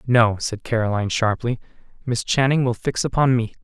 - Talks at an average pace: Yes, average, 165 wpm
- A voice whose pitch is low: Yes, low, 120 Hz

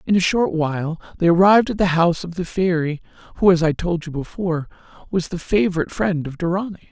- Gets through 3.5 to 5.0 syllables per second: No, 6.3 syllables/s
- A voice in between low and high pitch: Yes, medium, 175 Hz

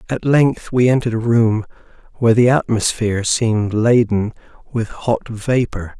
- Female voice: No, male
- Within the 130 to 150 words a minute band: Yes, average, 140 wpm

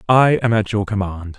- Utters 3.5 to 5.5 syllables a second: Yes, 5.0 syllables/s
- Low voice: Yes, low, 105 Hz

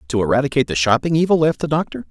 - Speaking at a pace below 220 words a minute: No, fast, 230 wpm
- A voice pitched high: No, medium, 140 Hz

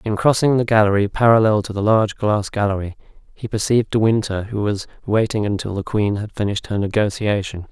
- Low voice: Yes, low, 105 Hz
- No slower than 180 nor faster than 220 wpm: Yes, average, 185 wpm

